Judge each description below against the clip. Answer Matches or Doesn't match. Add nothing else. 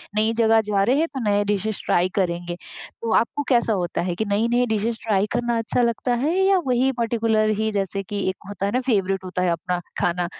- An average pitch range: Matches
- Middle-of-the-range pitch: Doesn't match